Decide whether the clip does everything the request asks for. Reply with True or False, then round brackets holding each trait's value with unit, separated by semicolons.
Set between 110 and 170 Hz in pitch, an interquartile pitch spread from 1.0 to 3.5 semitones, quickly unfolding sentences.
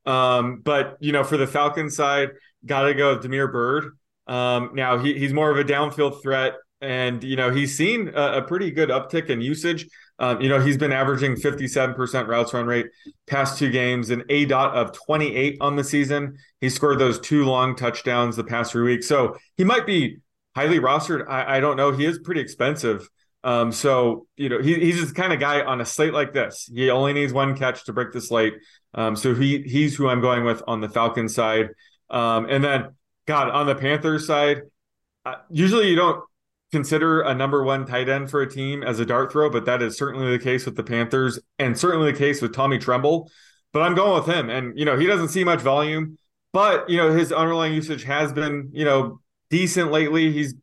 True (140 Hz; 3.0 semitones; 215 wpm)